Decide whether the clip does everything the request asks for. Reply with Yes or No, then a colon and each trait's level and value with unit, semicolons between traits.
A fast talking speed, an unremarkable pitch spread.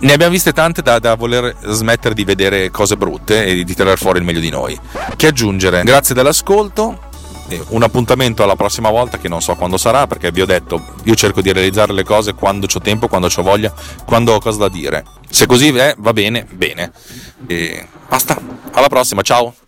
Yes: fast, 200 wpm; average, 4.1 semitones